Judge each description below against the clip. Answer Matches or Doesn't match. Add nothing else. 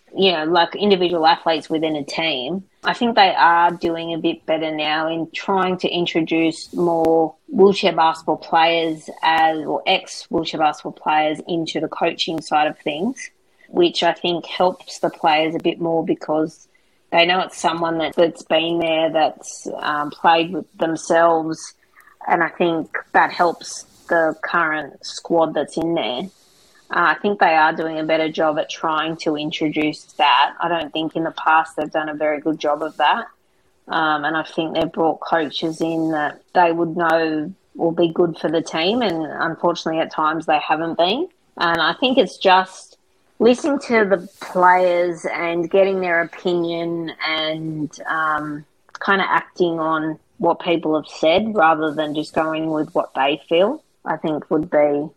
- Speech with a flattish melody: Matches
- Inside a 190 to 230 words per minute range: Doesn't match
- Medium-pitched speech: Matches